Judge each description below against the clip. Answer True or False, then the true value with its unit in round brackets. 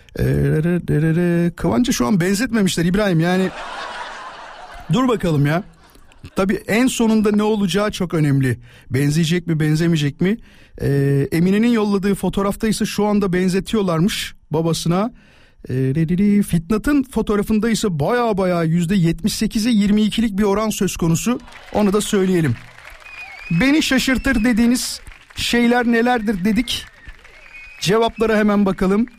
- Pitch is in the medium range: False (200 Hz)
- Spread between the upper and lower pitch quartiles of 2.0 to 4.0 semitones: False (4.4 semitones)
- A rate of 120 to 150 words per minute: False (105 wpm)